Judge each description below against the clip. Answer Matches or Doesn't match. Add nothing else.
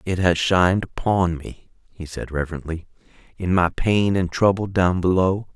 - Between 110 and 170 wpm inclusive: Matches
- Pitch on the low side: Matches